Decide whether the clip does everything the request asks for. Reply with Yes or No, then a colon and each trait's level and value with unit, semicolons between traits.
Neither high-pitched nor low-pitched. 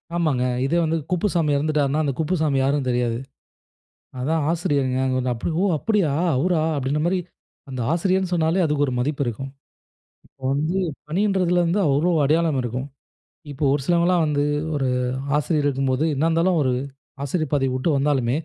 Yes: medium, 150 Hz